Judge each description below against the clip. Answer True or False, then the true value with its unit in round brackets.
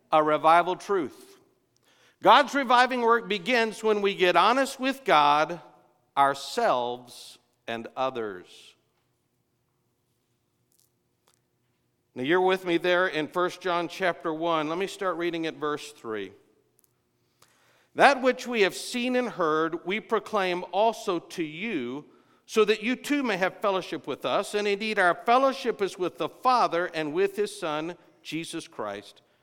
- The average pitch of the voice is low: False (180 Hz)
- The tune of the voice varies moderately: False (6.0 semitones)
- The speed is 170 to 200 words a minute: False (140 wpm)